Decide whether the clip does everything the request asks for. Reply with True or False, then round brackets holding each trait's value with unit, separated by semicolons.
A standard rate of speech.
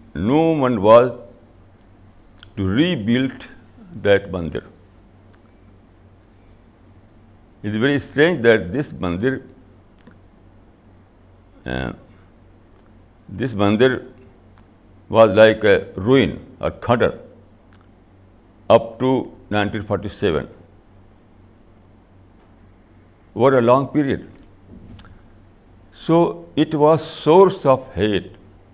False (75 wpm)